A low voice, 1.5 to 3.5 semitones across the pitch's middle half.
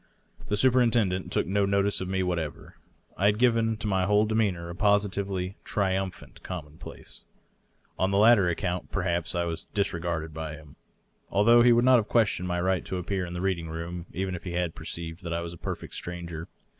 Yes: very low, 95 Hz; average, 3.0 semitones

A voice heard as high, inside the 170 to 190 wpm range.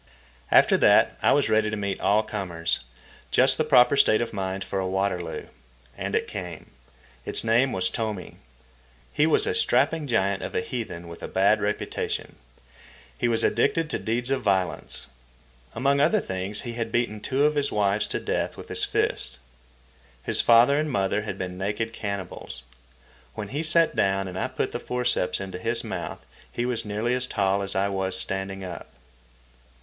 No: low, 105 Hz; average, 175 wpm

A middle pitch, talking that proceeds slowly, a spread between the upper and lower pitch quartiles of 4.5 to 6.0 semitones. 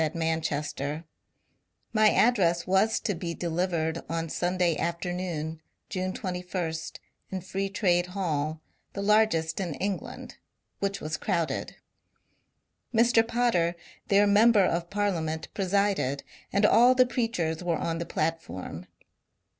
No: medium, 180 Hz; slow, 120 wpm; average, 3.7 semitones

